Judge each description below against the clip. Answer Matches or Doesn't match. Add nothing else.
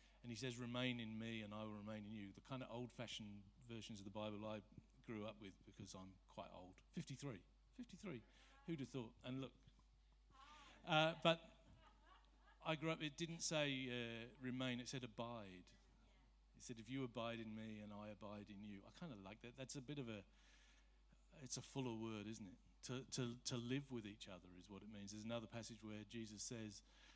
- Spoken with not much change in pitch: Doesn't match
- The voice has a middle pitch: Doesn't match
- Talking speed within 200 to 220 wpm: Matches